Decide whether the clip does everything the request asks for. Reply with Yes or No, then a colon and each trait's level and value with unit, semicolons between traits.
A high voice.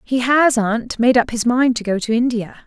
Yes: high, 240 Hz